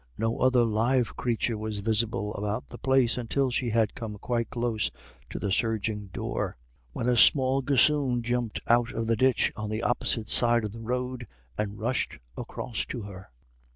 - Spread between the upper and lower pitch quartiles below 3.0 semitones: Yes, narrow, 2.4 semitones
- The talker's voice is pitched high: No, low, 115 Hz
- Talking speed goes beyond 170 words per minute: Yes, average, 180 wpm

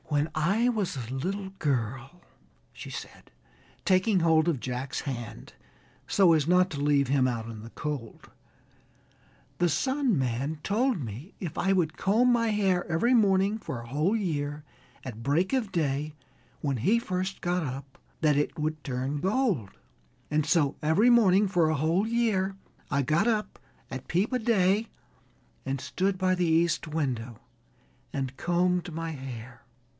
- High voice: No, medium, 160 Hz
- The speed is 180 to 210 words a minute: No, average, 160 wpm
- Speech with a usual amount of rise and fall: No, wide, 5.8 semitones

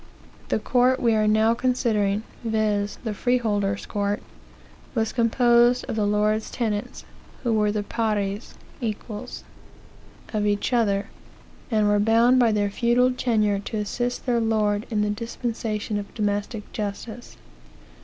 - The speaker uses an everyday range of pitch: No, narrow, 2.3 semitones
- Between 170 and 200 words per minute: No, slow, 135 wpm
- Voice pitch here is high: Yes, high, 215 Hz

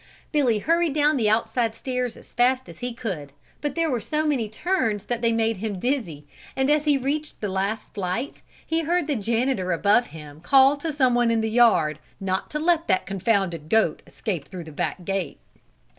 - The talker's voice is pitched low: No, high, 230 Hz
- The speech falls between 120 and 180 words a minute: No, average, 190 wpm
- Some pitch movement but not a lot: No, wide, 6.1 semitones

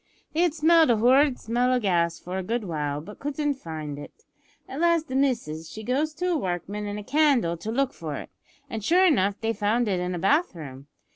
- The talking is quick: Yes, fast, 220 wpm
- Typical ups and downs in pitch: No, wide, 8.3 semitones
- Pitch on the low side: No, high, 225 Hz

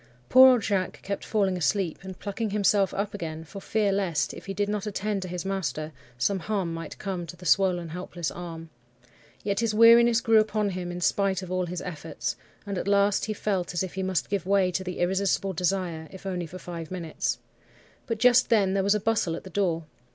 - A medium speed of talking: No, fast, 215 wpm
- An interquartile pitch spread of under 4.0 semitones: Yes, narrow, 2.5 semitones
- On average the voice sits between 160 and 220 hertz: Yes, high, 190 Hz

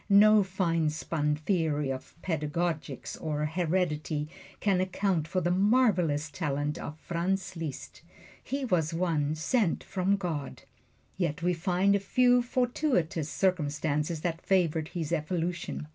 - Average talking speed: No, slow, 125 wpm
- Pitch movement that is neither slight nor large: Yes, average, 3.8 semitones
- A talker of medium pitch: Yes, medium, 170 Hz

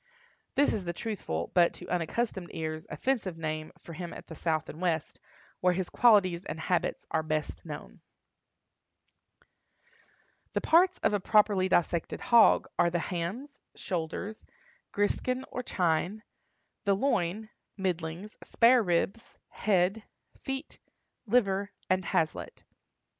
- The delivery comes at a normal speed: No, slow, 125 wpm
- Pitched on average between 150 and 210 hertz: Yes, medium, 185 Hz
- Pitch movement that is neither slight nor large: Yes, average, 4.4 semitones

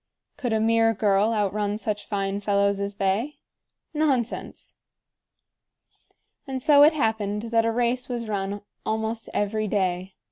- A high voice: Yes, high, 215 Hz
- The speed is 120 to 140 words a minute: Yes, slow, 135 wpm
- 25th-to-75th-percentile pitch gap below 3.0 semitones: Yes, narrow, 2.5 semitones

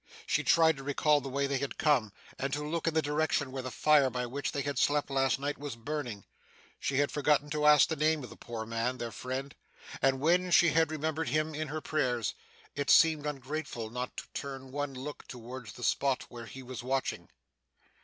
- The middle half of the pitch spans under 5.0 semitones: Yes, average, 2.8 semitones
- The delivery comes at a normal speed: No, fast, 215 wpm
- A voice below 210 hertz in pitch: Yes, medium, 140 Hz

